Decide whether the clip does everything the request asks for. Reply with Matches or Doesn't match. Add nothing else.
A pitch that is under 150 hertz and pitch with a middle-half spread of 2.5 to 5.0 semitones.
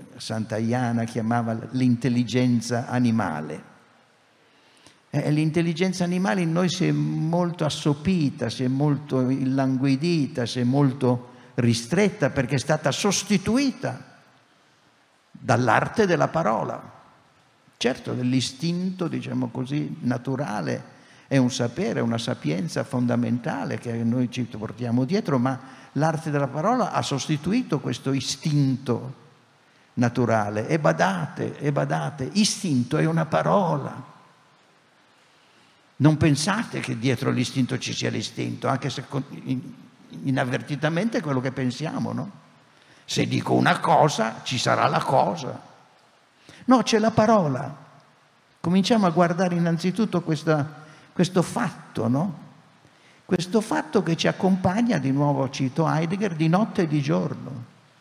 Doesn't match